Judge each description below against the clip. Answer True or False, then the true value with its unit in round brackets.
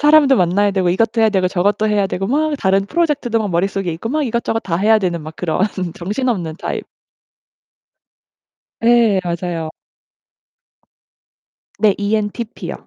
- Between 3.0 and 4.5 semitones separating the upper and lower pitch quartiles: True (4.1 semitones)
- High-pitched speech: True (205 Hz)